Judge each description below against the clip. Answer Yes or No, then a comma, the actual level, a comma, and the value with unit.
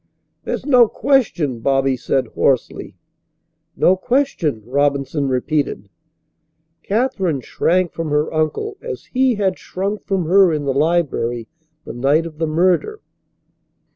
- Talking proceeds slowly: Yes, slow, 125 wpm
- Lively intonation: Yes, wide, 6.1 semitones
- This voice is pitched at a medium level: Yes, medium, 160 Hz